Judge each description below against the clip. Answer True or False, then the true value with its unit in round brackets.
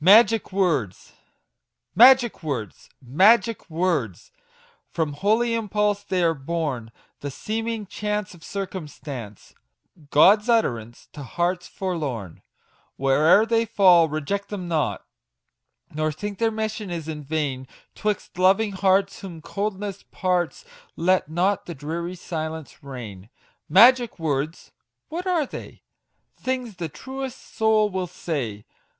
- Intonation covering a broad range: True (5.7 semitones)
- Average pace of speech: False (120 wpm)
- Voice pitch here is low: False (180 Hz)